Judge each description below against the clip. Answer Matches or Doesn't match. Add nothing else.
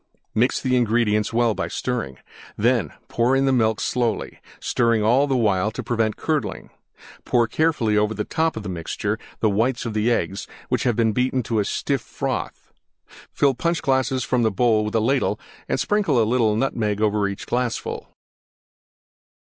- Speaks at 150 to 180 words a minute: Matches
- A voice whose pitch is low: Matches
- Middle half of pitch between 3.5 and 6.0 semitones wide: Doesn't match